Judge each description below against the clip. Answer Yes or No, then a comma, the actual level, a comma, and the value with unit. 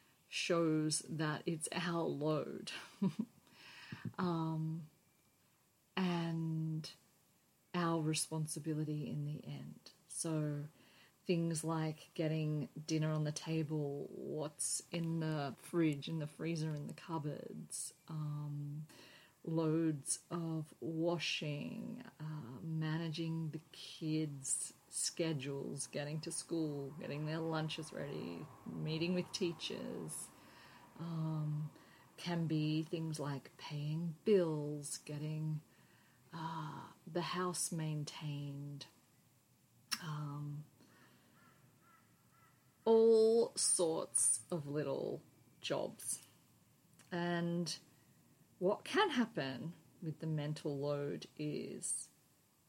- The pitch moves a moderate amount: No, narrow, 2.0 semitones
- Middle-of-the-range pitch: Yes, medium, 160 Hz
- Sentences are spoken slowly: Yes, slow, 85 wpm